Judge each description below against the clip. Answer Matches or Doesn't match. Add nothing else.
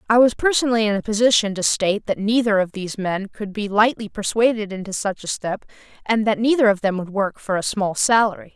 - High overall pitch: Matches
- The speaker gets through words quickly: Matches